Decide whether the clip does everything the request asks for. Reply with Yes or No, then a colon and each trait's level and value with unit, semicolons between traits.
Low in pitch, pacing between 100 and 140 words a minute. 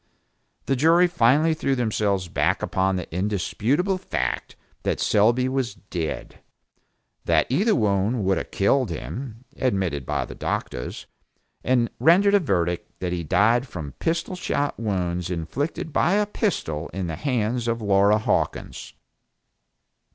Yes: low, 110 Hz; slow, 135 wpm